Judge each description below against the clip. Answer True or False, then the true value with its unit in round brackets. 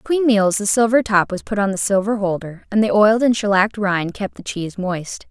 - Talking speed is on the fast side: True (235 wpm)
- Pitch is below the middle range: False (205 Hz)